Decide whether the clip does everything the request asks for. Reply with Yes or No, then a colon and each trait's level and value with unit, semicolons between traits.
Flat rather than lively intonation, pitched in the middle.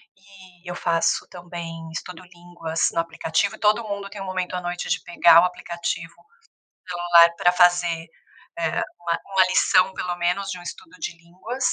Yes: narrow, 1.9 semitones; medium, 175 Hz